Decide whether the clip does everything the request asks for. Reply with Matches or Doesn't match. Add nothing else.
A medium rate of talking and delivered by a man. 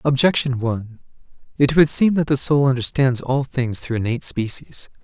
Matches